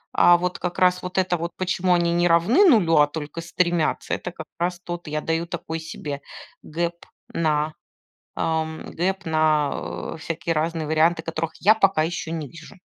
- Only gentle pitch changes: Yes, narrow, 1.9 semitones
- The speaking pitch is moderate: Yes, medium, 165 Hz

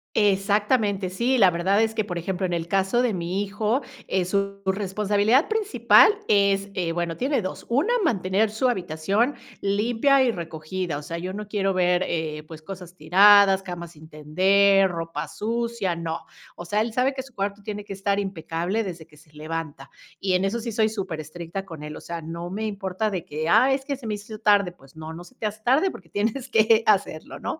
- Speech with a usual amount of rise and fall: Yes, average, 4.0 semitones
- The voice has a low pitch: No, high, 195 Hz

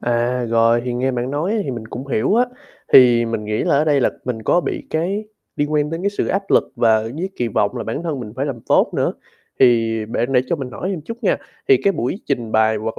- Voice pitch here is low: Yes, low, 125 Hz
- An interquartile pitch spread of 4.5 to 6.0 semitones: Yes, wide, 5.5 semitones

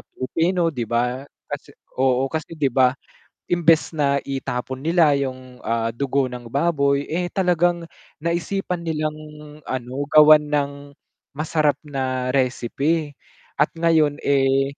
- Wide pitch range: No, average, 3.8 semitones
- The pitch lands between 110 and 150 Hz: Yes, medium, 140 Hz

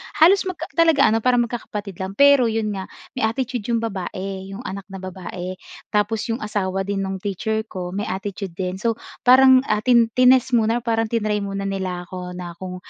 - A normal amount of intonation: Yes, average, 3.8 semitones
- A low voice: No, high, 210 Hz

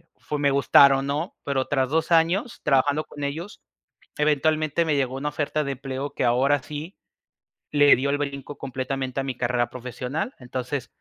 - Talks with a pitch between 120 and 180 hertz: Yes, medium, 140 Hz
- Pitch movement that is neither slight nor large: No, narrow, 2.2 semitones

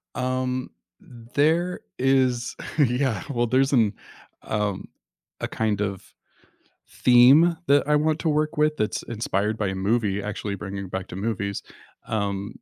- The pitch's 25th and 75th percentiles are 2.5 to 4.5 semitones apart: No, wide, 5.4 semitones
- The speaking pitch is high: No, low, 120 Hz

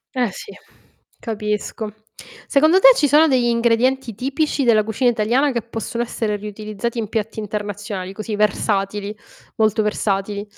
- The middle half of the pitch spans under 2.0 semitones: No, narrow, 2.6 semitones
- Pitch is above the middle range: Yes, high, 220 Hz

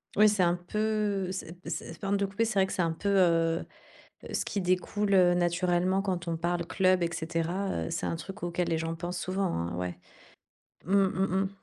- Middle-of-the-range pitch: Yes, medium, 180 Hz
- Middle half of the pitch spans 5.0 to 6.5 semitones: No, narrow, 2.4 semitones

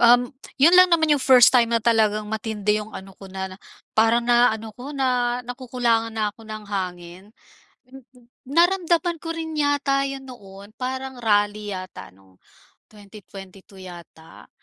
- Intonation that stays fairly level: No, average, 4.5 semitones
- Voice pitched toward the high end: Yes, high, 230 Hz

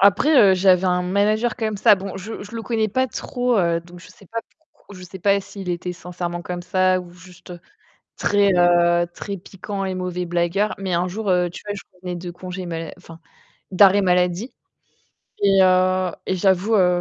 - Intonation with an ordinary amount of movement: No, narrow, 2.1 semitones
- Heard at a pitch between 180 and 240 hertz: Yes, medium, 185 Hz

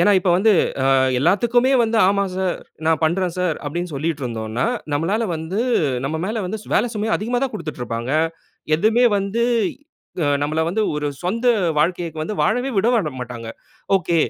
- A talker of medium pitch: Yes, medium, 180 Hz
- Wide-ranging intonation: Yes, wide, 5.8 semitones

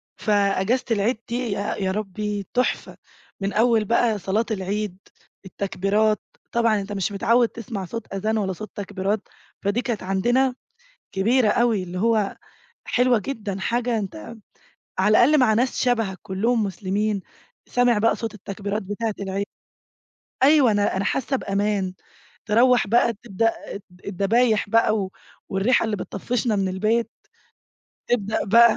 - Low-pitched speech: No, high, 215 Hz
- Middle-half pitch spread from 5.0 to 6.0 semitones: No, average, 2.9 semitones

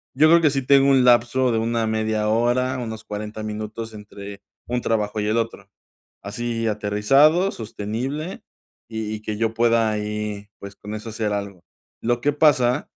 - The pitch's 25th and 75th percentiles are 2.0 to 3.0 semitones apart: Yes, narrow, 2.6 semitones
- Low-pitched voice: Yes, low, 115 Hz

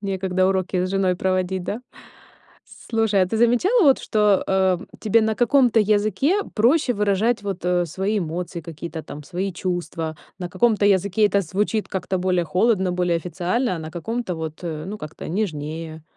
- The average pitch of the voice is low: No, high, 190 Hz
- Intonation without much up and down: No, average, 3.4 semitones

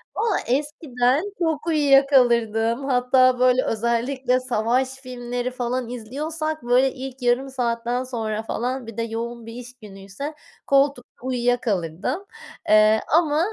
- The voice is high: Yes, very high, 250 Hz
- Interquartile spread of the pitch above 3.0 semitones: No, narrow, 2.5 semitones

